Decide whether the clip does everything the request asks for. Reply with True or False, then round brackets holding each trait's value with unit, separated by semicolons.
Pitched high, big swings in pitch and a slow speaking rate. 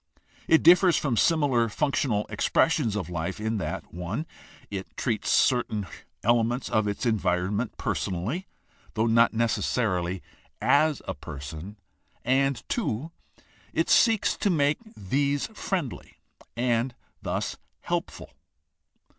False (115 Hz; 5.7 semitones; 115 wpm)